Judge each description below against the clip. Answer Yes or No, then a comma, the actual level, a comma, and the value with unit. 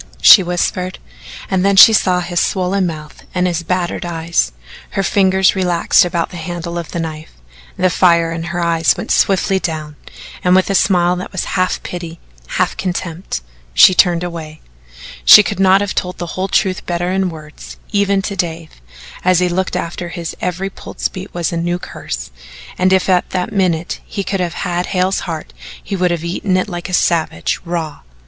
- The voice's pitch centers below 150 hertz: No, medium, 180 Hz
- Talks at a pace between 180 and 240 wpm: Yes, average, 195 wpm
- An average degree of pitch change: No, narrow, 1.8 semitones